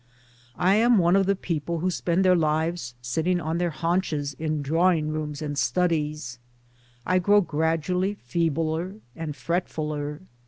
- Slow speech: No, average, 145 wpm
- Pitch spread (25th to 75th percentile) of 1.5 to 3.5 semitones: Yes, average, 3.1 semitones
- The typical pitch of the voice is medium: Yes, medium, 165 Hz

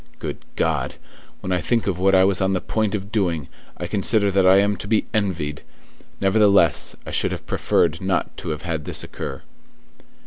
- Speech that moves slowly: No, average, 195 wpm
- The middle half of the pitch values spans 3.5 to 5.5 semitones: No, average, 3.0 semitones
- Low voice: Yes, very low, 95 Hz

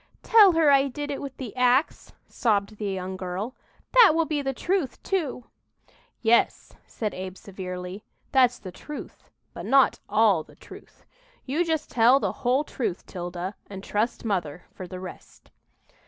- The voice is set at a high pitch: Yes, high, 235 Hz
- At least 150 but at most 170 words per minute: Yes, average, 160 wpm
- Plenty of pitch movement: Yes, wide, 6.8 semitones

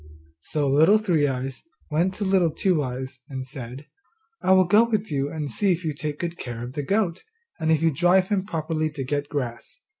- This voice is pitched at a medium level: Yes, medium, 155 Hz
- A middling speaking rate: No, fast, 210 wpm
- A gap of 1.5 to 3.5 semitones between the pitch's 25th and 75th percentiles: No, average, 5.2 semitones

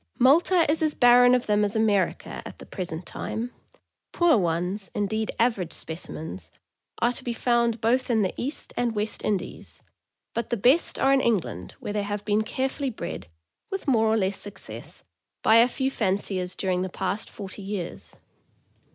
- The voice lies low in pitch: No, high, 220 Hz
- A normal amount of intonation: Yes, average, 4.2 semitones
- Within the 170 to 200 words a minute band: Yes, average, 175 wpm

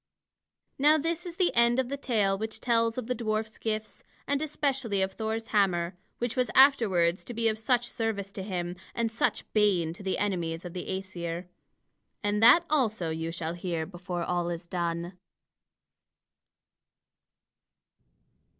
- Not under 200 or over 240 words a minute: No, average, 155 wpm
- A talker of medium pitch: No, high, 210 Hz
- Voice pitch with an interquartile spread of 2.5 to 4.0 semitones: No, average, 5.1 semitones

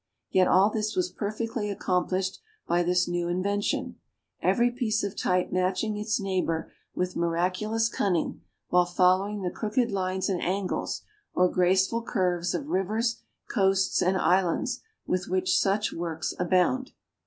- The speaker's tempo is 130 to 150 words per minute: Yes, average, 140 wpm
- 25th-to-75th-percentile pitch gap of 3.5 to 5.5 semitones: No, average, 2.7 semitones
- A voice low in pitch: No, high, 190 Hz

